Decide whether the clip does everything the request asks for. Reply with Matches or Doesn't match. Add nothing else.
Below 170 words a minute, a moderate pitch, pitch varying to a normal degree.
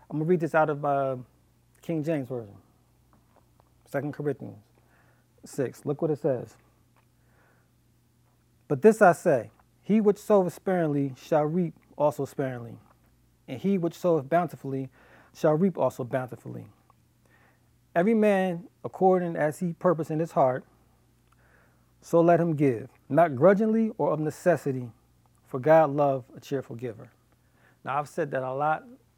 Matches